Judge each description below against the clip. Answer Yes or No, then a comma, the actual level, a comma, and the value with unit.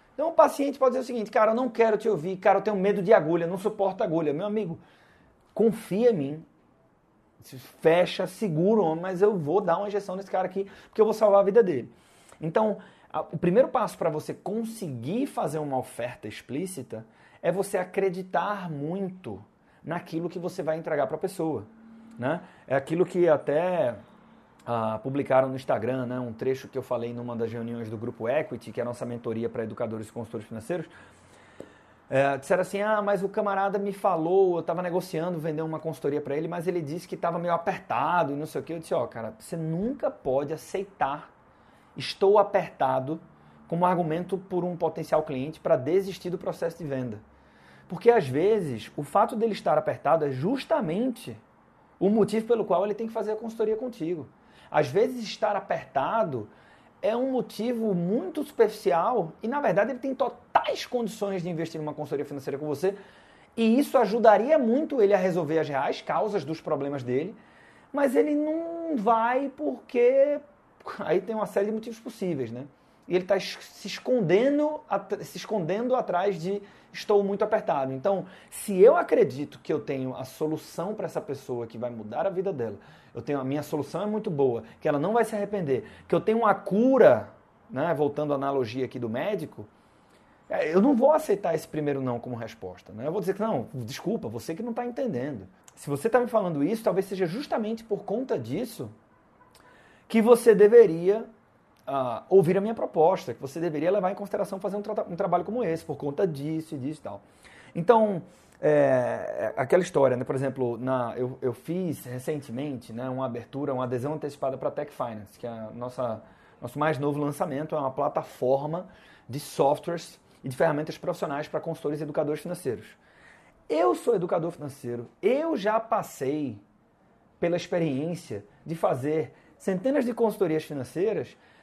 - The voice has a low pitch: No, medium, 175 Hz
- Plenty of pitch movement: Yes, wide, 6.9 semitones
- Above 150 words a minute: Yes, average, 180 wpm